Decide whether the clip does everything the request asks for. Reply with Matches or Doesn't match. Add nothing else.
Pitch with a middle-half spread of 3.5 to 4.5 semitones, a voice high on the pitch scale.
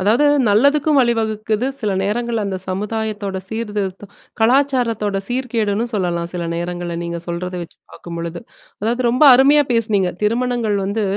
Matches